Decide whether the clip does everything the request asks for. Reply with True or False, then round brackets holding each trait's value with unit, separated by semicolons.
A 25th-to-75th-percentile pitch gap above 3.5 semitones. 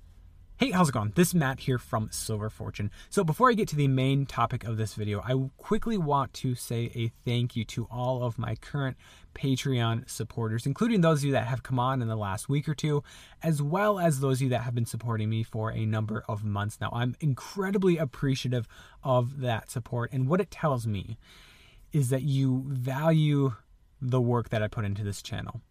True (3.9 semitones)